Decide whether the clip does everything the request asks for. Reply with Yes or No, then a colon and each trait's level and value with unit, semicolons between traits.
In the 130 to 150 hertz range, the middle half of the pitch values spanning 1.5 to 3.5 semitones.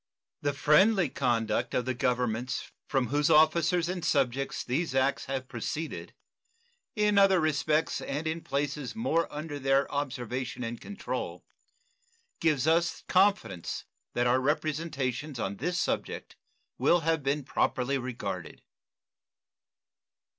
No: medium, 140 Hz; average, 4.3 semitones